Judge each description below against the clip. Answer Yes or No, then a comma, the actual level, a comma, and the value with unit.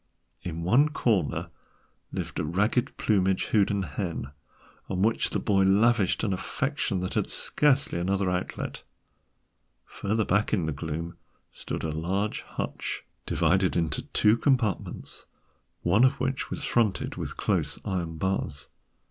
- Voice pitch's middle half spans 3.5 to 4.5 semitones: Yes, average, 4.1 semitones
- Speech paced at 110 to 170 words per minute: Yes, slow, 135 wpm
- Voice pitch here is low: Yes, very low, 95 Hz